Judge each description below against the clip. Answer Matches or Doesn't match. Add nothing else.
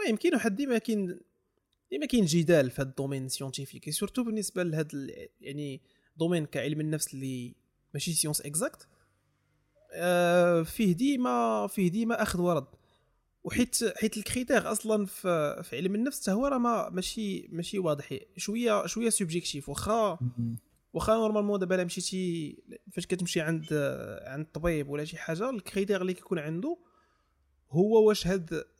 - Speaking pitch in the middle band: Matches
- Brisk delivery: Matches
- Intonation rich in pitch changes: Matches